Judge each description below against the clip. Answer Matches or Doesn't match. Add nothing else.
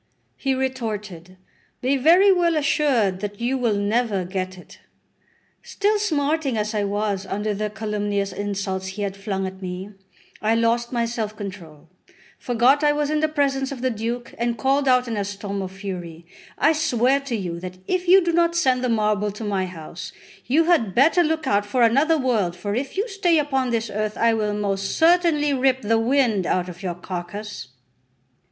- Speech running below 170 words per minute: Doesn't match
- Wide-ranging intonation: Matches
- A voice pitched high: Matches